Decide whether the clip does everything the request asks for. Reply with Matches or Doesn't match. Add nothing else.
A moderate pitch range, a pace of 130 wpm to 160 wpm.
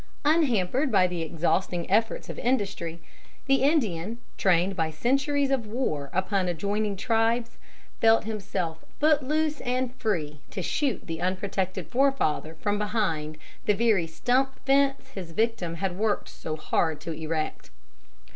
Doesn't match